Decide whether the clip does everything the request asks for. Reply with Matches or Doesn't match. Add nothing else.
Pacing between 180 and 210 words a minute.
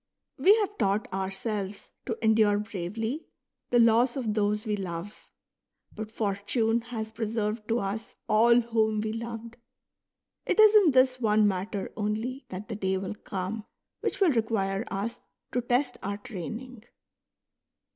Doesn't match